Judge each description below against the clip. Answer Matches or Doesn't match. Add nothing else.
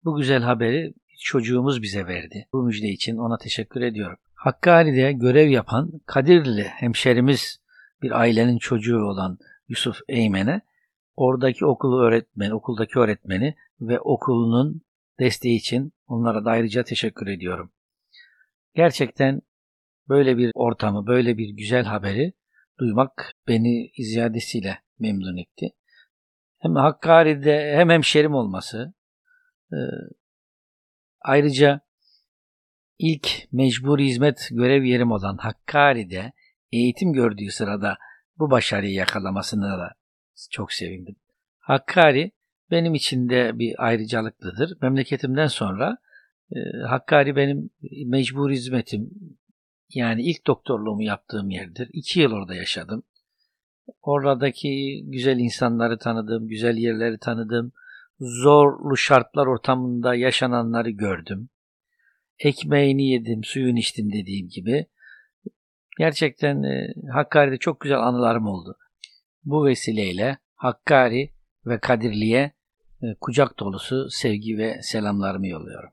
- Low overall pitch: Matches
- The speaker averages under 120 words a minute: Matches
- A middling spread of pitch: Matches